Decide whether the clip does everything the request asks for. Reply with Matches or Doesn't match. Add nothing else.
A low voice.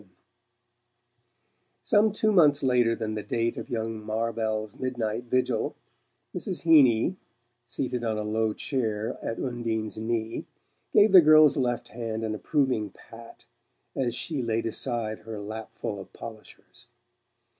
Matches